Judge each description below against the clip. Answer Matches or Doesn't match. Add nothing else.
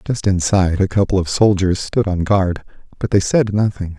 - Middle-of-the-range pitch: Doesn't match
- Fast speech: Doesn't match